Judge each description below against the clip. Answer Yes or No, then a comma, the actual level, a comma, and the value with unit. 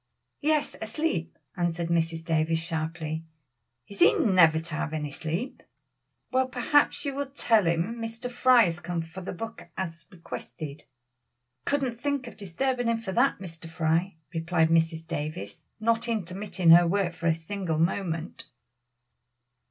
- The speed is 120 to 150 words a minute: Yes, average, 145 wpm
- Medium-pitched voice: Yes, medium, 175 Hz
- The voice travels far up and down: Yes, wide, 5.8 semitones